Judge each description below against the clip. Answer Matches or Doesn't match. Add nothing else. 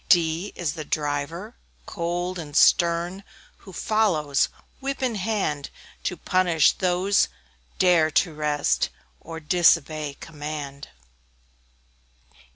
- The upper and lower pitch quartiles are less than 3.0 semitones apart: Doesn't match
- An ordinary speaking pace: Doesn't match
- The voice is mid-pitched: Matches